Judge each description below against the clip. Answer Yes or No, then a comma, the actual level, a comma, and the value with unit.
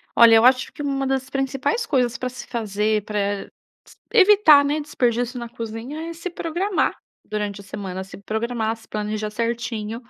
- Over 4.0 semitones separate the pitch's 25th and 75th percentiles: Yes, average, 4.7 semitones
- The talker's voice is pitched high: Yes, high, 235 Hz